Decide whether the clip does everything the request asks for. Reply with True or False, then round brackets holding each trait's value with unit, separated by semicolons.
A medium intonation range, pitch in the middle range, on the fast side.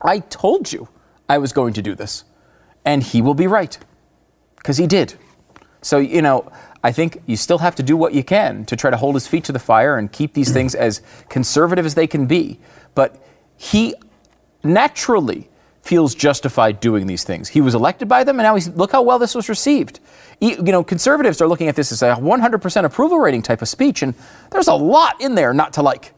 False (7.8 semitones; 150 Hz; 220 wpm)